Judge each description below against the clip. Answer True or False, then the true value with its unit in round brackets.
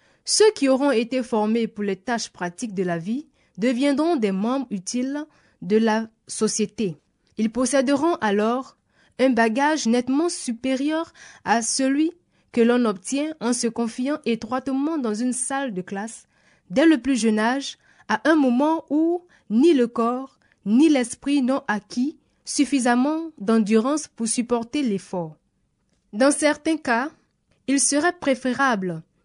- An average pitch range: True (4.2 semitones)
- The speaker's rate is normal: False (135 wpm)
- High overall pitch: True (250 Hz)